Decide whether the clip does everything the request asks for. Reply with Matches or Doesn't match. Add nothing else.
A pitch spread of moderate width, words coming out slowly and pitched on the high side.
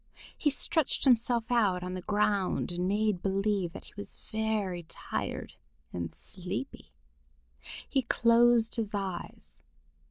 Matches